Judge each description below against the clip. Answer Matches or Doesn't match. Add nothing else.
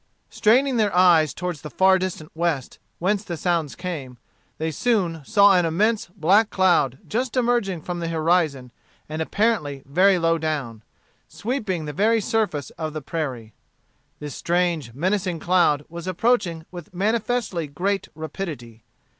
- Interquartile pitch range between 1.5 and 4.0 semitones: Doesn't match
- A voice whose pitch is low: Doesn't match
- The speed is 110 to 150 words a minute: Matches